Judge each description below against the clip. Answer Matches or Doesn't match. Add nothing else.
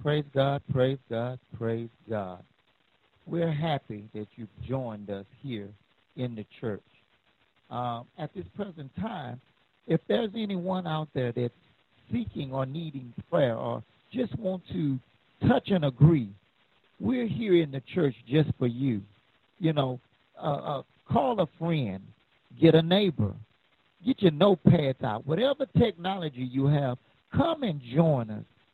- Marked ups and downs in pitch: Matches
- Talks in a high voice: Doesn't match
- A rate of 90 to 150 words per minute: Matches